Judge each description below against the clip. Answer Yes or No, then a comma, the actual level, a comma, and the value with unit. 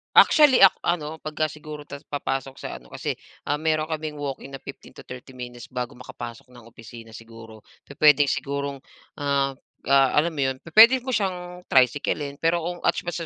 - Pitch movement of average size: Yes, average, 3.5 semitones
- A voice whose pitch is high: No, medium, 145 Hz